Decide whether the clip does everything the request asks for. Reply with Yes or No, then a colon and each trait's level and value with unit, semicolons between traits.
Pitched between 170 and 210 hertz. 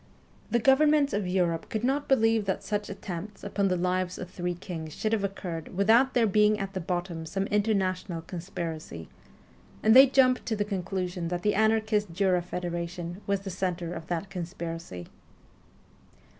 Yes: high, 190 Hz